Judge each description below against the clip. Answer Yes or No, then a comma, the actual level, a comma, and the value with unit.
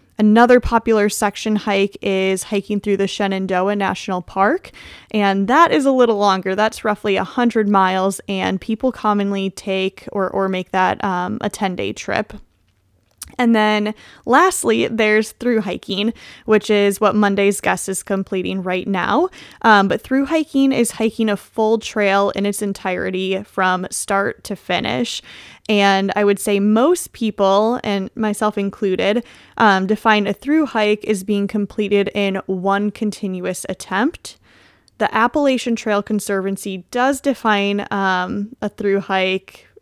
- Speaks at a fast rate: No, average, 145 wpm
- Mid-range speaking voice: No, high, 205 Hz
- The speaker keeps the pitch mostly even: Yes, narrow, 2.3 semitones